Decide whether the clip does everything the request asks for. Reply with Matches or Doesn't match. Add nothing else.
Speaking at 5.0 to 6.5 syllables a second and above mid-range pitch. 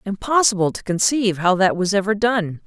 Matches